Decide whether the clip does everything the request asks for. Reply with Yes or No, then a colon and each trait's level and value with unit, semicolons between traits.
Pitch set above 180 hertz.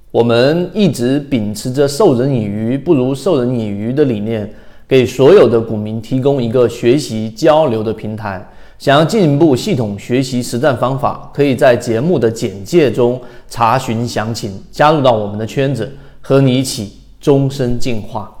No: low, 125 Hz